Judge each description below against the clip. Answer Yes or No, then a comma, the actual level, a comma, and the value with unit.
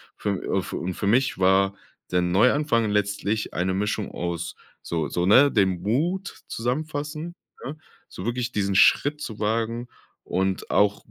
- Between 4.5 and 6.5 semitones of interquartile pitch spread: Yes, average, 4.9 semitones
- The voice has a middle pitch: No, low, 105 Hz